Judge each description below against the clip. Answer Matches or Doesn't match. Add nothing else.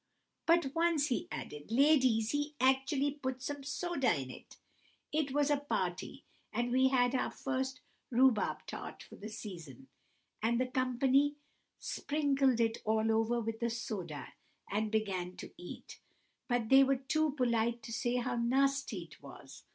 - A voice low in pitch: Doesn't match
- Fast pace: Doesn't match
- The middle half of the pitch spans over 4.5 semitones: Doesn't match